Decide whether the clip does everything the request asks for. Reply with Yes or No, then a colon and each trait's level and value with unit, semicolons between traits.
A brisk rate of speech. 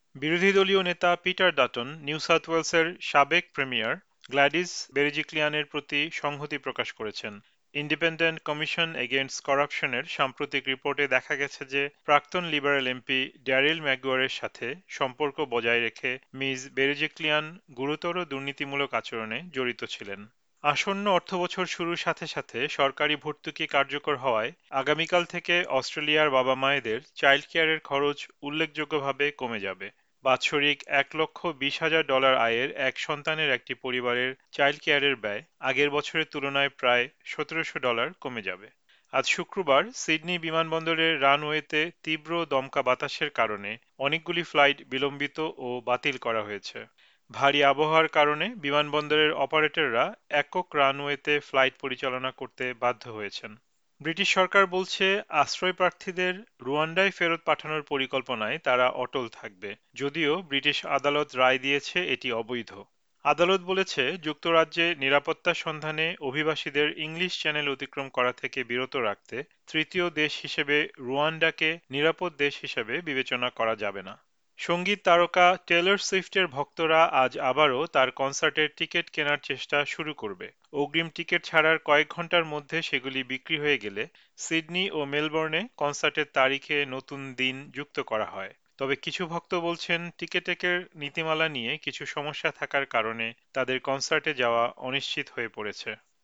Yes: fast, 125 wpm